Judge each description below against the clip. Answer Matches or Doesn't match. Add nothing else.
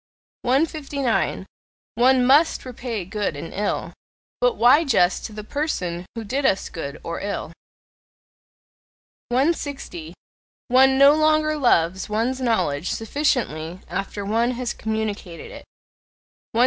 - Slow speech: Matches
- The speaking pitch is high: Matches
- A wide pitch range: Matches